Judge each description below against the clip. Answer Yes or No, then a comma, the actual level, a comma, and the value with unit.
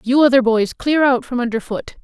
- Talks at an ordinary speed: No, fast, 235 wpm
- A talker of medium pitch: No, very high, 250 Hz